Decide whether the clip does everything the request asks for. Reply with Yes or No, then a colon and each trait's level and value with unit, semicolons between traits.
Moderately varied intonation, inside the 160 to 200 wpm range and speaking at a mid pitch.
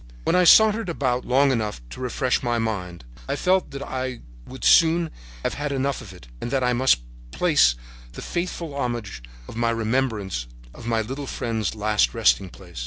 No: average, 4.3 semitones; average, 185 wpm; low, 125 Hz